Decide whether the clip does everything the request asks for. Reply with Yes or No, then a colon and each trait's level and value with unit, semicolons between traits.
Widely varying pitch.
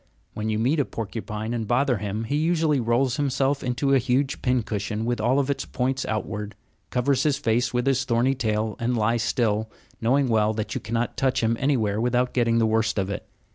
No: average, 3.3 semitones